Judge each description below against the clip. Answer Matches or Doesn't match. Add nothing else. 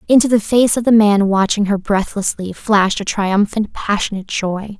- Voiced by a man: Doesn't match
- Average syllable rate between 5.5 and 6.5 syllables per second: Doesn't match